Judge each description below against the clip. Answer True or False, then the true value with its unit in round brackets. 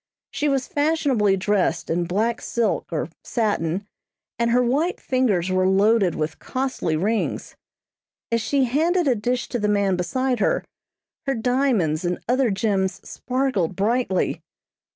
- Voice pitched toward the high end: True (225 Hz)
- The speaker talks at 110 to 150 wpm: True (140 wpm)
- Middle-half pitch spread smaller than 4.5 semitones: False (5.2 semitones)